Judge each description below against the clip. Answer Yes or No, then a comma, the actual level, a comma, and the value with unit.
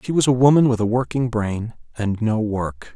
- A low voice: Yes, low, 115 Hz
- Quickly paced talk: Yes, fast, 225 wpm